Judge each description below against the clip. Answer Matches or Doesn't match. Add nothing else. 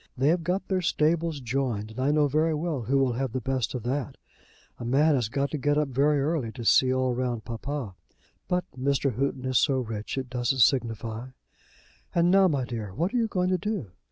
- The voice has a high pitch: Doesn't match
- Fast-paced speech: Matches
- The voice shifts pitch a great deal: Doesn't match